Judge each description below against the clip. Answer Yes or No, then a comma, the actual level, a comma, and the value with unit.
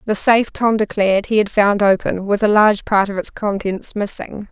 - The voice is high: Yes, high, 205 Hz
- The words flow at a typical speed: No, fast, 210 wpm